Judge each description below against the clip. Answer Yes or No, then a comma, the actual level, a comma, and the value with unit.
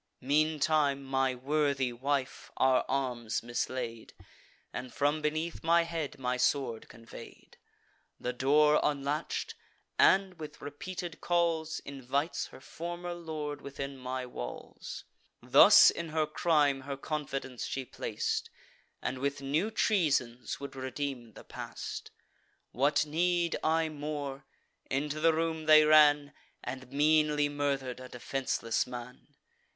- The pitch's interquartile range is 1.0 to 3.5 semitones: Yes, average, 2.9 semitones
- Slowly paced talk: Yes, slow, 120 wpm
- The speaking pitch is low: No, medium, 145 Hz